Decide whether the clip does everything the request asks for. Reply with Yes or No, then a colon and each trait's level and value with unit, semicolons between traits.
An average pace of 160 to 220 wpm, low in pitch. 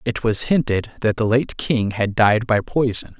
Yes: fast, 205 wpm; low, 115 Hz